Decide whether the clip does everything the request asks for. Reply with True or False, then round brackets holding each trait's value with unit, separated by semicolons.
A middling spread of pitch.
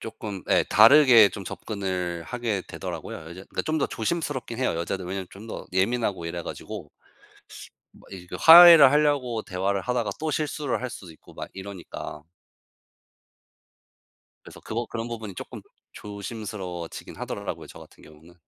True (5.0 semitones)